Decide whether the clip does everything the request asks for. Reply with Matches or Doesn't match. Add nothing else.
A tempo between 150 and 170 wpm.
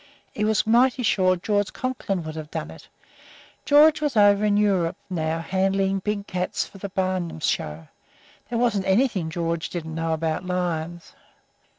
Matches